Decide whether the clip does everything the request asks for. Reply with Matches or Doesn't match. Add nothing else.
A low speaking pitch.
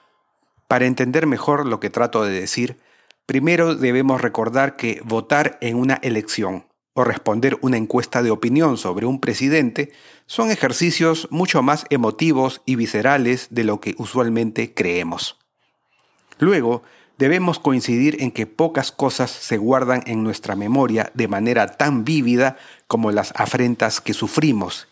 Matches